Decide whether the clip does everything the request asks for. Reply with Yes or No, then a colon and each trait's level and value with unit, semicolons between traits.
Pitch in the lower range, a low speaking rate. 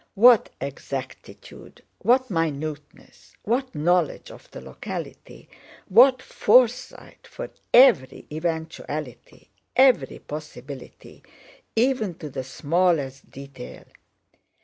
No: medium, 170 Hz; slow, 85 wpm